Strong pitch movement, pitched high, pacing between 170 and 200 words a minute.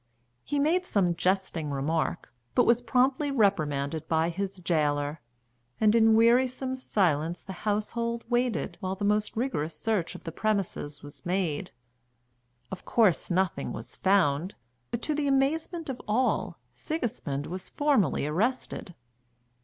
No: wide, 6.9 semitones; high, 200 Hz; slow, 135 wpm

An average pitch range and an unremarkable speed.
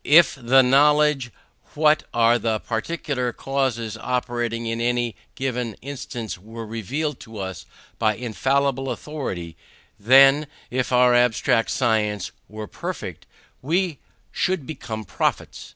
No: average, 3.4 semitones; slow, 120 wpm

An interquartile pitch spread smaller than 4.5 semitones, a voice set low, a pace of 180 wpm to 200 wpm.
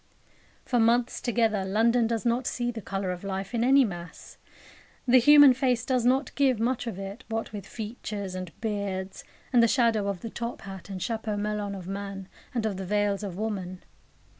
No: average, 3.5 semitones; high, 215 Hz; average, 190 wpm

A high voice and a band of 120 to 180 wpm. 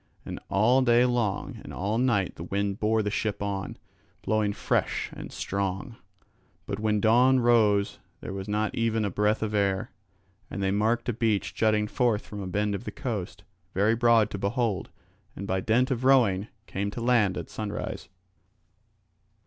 No: low, 105 Hz; average, 175 wpm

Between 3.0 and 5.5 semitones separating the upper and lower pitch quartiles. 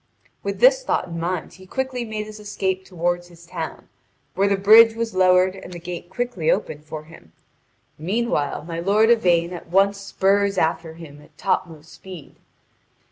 Yes: average, 3.3 semitones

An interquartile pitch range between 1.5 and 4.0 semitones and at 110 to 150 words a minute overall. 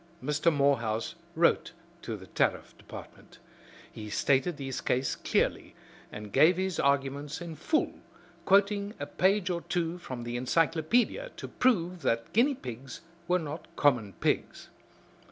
No: wide, 5.6 semitones; slow, 135 wpm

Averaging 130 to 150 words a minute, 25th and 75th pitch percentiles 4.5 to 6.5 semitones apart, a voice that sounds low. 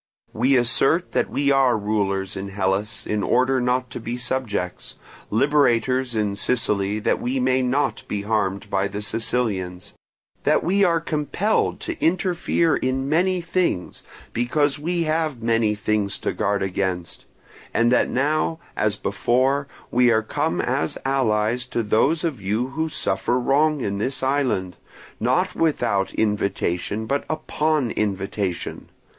Yes: average, 140 wpm; wide, 5.5 semitones; low, 120 Hz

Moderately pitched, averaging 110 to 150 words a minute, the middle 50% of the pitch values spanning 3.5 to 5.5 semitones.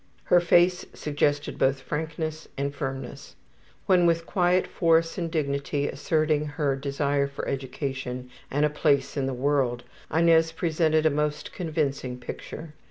No: medium, 150 Hz; average, 140 wpm; average, 2.7 semitones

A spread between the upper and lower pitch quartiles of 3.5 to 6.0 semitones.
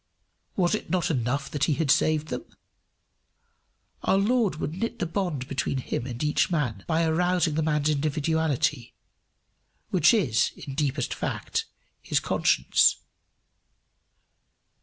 Yes: average, 3.8 semitones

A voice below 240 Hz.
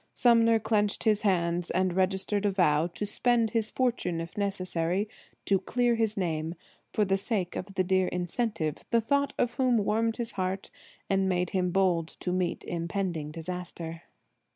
Yes: high, 190 Hz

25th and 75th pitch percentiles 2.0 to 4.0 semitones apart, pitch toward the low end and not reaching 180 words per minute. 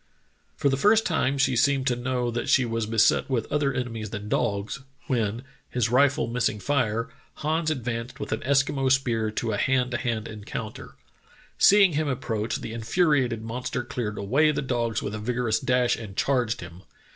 No: average, 3.2 semitones; low, 120 Hz; average, 185 wpm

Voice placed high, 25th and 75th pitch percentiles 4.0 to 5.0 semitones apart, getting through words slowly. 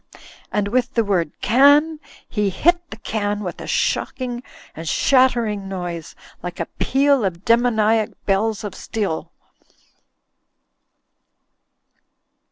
Yes: high, 220 Hz; average, 4.4 semitones; slow, 115 wpm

